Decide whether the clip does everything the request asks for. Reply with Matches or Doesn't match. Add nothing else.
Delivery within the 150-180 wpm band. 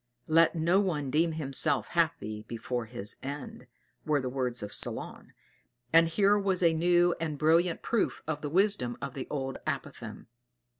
Matches